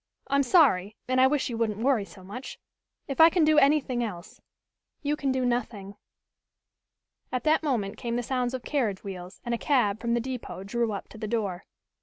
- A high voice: Yes, high, 240 Hz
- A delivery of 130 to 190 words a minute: No, fast, 205 wpm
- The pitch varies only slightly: No, average, 4.4 semitones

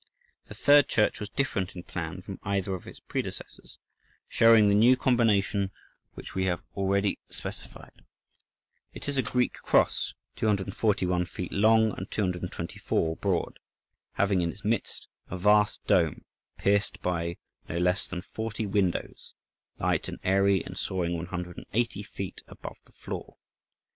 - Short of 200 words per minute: Yes, average, 140 wpm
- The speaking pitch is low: Yes, low, 100 Hz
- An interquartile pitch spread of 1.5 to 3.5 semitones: Yes, average, 2.8 semitones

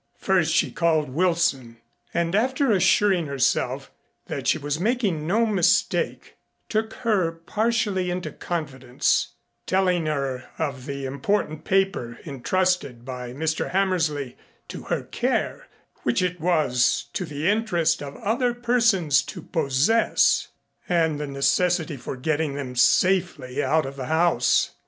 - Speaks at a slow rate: Yes, slow, 130 wpm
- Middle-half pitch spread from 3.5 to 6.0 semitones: Yes, wide, 5.4 semitones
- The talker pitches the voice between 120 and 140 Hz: No, medium, 165 Hz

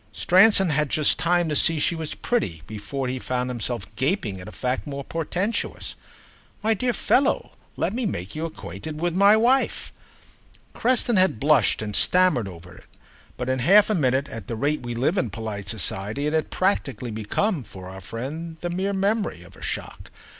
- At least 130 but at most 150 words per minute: No, average, 185 wpm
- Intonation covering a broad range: Yes, wide, 8.5 semitones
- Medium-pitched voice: Yes, medium, 150 Hz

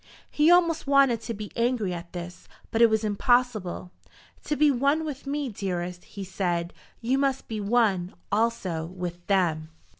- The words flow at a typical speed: Yes, average, 160 wpm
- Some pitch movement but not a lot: No, wide, 6.6 semitones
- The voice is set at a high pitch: Yes, high, 215 Hz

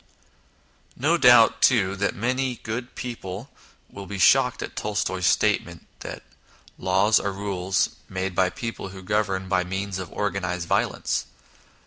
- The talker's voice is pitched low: Yes, low, 100 Hz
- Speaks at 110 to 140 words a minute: Yes, slow, 135 wpm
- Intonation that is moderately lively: Yes, average, 3.5 semitones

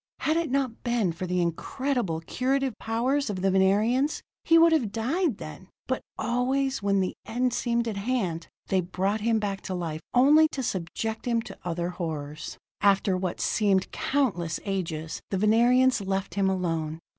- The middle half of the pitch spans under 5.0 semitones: No, wide, 5.6 semitones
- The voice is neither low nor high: No, high, 205 Hz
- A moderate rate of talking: Yes, average, 170 wpm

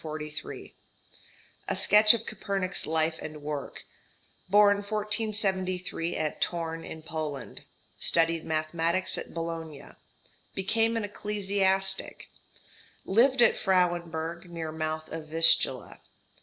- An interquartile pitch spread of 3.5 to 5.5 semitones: Yes, average, 3.9 semitones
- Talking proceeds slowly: Yes, slow, 100 wpm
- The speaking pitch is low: No, medium, 175 Hz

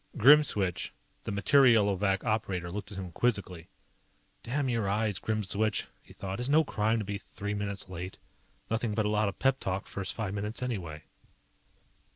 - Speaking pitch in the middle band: No, low, 105 Hz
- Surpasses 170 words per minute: No, average, 165 wpm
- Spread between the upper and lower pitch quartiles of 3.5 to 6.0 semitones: No, average, 2.9 semitones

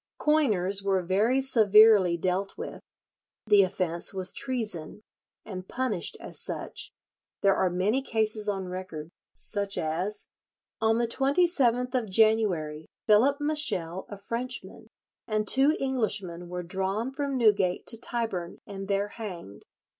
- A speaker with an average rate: No, slow, 125 wpm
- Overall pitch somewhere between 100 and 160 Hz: No, high, 210 Hz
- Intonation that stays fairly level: No, average, 4.6 semitones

